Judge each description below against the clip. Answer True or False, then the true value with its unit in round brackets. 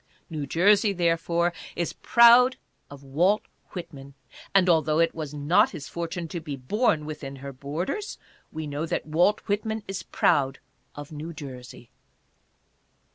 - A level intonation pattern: False (4.2 semitones)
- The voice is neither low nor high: True (165 Hz)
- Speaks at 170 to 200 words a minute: False (140 wpm)